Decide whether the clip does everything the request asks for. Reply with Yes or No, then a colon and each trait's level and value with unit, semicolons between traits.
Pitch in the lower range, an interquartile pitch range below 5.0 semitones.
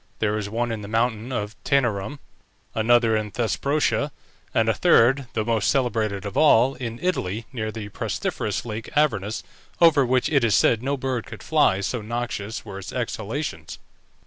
Yes: low, 115 Hz; average, 3.3 semitones